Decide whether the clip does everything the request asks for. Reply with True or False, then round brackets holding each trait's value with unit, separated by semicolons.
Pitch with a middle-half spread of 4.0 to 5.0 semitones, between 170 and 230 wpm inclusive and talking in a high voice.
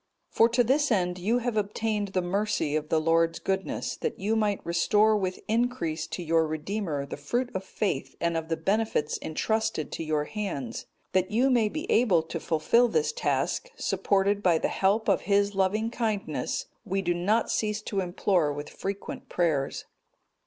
True (4.7 semitones; 180 wpm; 195 Hz)